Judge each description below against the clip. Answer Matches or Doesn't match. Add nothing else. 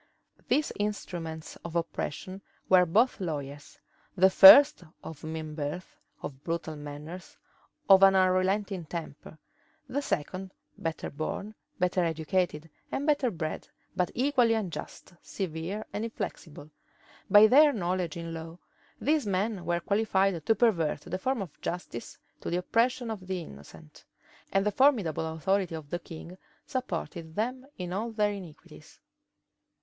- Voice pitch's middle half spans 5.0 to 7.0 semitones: Doesn't match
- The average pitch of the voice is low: Doesn't match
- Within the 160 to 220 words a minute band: Doesn't match